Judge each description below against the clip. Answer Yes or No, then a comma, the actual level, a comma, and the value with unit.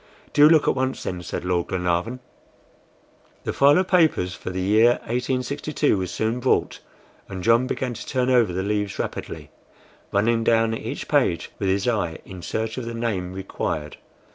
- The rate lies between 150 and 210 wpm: Yes, average, 170 wpm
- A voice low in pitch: Yes, low, 115 Hz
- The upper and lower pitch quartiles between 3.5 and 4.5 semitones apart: No, average, 5.3 semitones